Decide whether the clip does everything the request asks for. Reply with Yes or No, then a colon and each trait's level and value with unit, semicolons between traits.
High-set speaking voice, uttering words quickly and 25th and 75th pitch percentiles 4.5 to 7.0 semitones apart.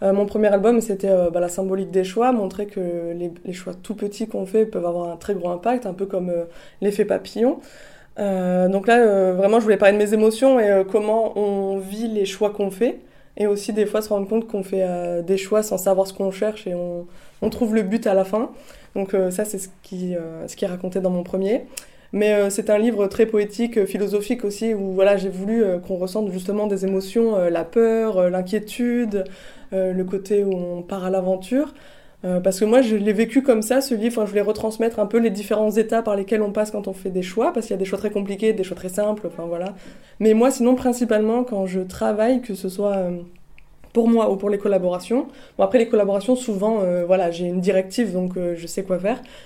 No: high, 205 Hz; fast, 240 wpm; average, 2.8 semitones